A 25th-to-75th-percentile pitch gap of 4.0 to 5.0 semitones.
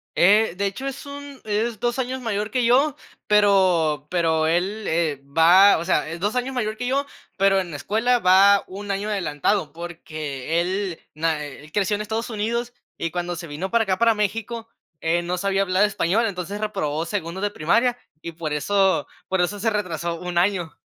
Yes: average, 4.4 semitones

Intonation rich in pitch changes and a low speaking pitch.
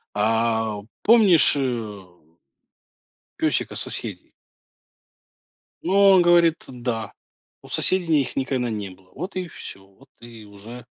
Yes: wide, 7.3 semitones; low, 120 Hz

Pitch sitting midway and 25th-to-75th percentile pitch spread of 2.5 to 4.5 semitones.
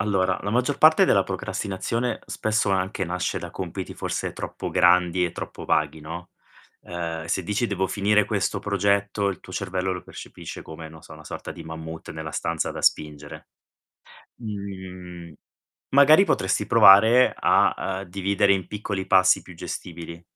No: very low, 95 Hz; average, 2.9 semitones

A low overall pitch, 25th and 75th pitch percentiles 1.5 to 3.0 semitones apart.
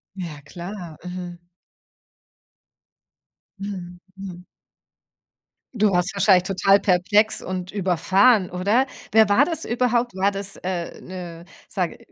No: high, 190 Hz; narrow, 2.4 semitones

